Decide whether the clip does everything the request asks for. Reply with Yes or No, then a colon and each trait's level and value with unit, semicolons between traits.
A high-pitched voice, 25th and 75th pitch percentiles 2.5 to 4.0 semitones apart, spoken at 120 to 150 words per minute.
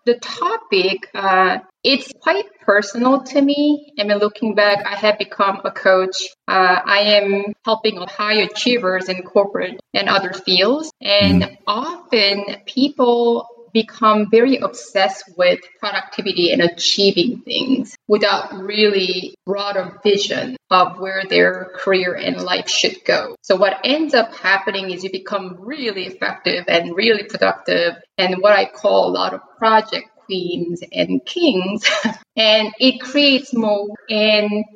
Yes: high, 205 Hz; average, 3.7 semitones; average, 140 wpm